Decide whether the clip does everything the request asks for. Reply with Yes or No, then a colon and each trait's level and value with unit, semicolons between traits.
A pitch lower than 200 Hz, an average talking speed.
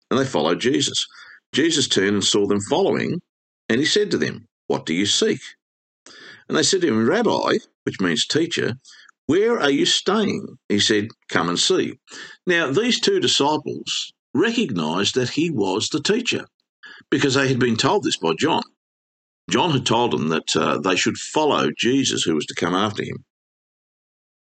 Yes: low, 135 Hz; average, 175 wpm